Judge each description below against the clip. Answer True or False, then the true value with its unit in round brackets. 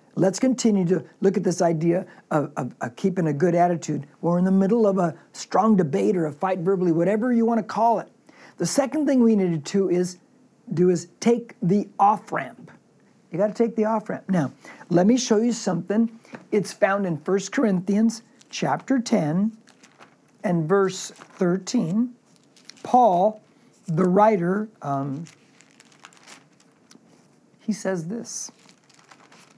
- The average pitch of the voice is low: False (200 Hz)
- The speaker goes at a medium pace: True (145 wpm)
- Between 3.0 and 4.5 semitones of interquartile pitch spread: True (3.9 semitones)